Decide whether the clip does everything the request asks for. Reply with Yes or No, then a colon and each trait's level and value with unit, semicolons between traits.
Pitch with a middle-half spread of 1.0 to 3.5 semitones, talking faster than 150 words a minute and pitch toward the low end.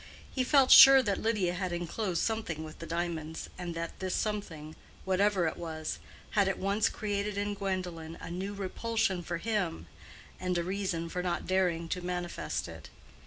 No: average, 3.2 semitones; average, 170 wpm; medium, 185 Hz